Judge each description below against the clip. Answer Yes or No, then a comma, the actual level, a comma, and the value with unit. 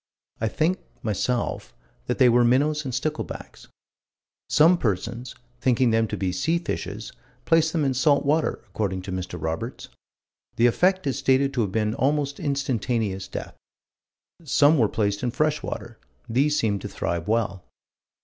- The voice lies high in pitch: No, low, 125 Hz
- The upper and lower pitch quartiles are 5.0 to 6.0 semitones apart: Yes, wide, 5.5 semitones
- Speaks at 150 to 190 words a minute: Yes, average, 155 wpm